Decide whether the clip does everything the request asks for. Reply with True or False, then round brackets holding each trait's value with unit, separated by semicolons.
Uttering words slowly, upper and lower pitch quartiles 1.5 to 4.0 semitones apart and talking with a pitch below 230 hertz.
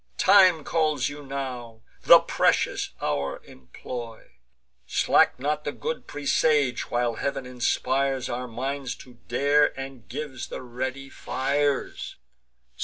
True (115 wpm; 2.8 semitones; 135 Hz)